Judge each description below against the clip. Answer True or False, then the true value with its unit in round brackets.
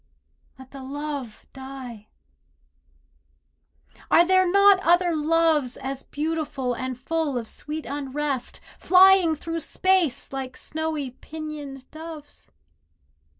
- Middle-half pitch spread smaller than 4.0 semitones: True (3.6 semitones)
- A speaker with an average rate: False (105 wpm)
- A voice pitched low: False (300 Hz)